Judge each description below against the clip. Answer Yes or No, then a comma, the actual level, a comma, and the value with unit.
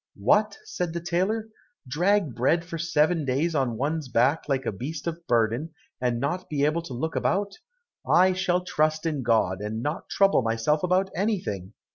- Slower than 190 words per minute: Yes, average, 175 wpm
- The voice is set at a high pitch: No, medium, 155 Hz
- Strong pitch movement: Yes, wide, 5.8 semitones